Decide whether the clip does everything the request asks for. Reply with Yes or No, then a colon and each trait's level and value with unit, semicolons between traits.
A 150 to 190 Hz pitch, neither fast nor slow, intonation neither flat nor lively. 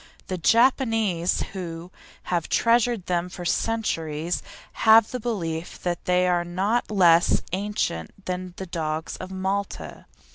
No: medium, 185 Hz; slow, 130 wpm; average, 3.7 semitones